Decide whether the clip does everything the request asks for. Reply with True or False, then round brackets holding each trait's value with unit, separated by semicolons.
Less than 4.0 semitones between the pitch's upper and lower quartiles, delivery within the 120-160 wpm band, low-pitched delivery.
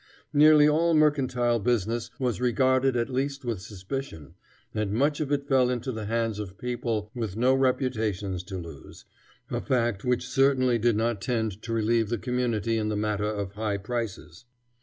False (3.4 semitones; 170 wpm; 115 Hz)